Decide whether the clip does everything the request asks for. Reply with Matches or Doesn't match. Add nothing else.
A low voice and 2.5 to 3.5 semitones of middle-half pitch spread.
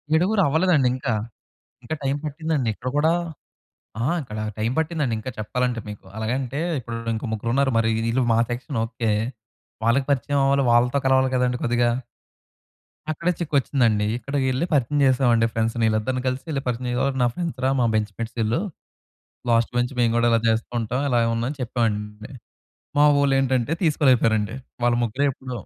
Matches